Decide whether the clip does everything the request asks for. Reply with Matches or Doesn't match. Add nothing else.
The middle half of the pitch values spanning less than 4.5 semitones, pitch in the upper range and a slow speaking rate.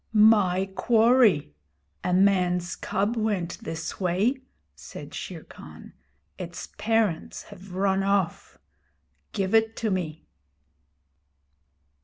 Matches